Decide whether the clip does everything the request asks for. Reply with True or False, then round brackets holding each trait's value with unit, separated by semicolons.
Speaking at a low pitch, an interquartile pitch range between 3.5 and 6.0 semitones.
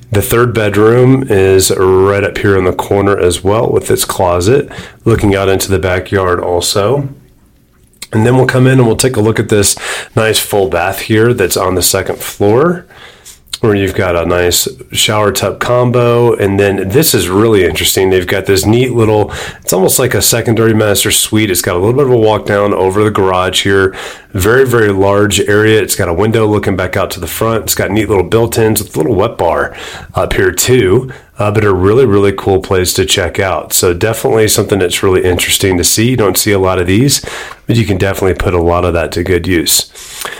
False (100 Hz; 2.9 semitones)